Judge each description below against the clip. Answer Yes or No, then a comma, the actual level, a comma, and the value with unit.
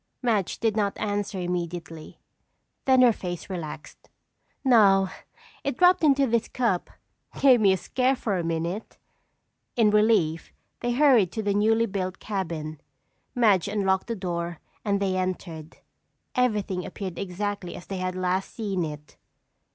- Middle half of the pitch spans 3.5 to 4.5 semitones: Yes, average, 4.0 semitones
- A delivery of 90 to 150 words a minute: Yes, average, 145 wpm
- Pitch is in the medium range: No, high, 195 Hz